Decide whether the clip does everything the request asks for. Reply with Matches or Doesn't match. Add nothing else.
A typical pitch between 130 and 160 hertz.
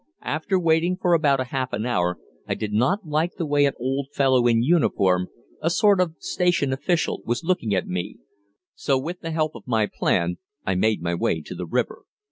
Matches